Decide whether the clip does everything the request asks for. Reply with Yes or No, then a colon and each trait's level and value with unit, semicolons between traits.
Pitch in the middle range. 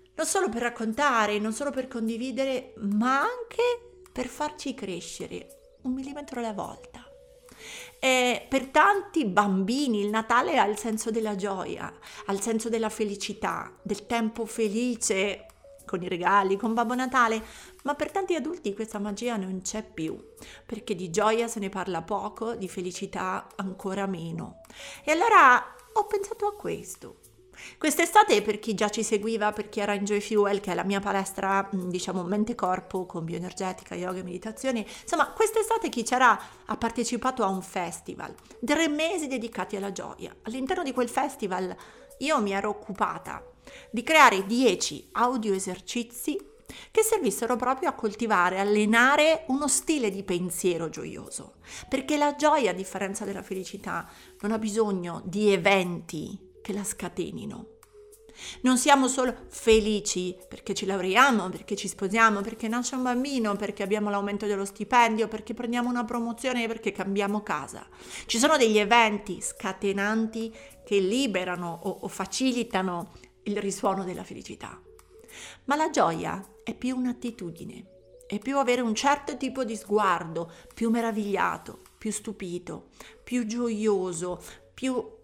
No: high, 220 Hz